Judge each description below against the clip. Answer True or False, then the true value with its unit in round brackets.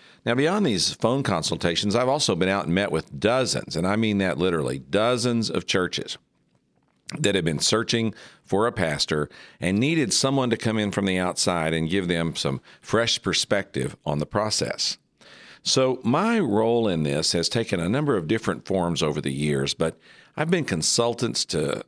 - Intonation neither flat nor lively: False (6.0 semitones)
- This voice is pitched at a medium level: False (95 Hz)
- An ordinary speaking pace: True (180 wpm)